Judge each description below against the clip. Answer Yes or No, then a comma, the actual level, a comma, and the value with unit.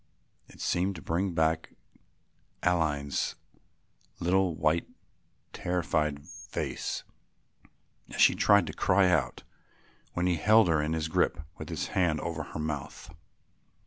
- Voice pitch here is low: Yes, very low, 80 Hz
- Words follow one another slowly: Yes, slow, 125 wpm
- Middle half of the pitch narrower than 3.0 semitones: Yes, narrow, 2.6 semitones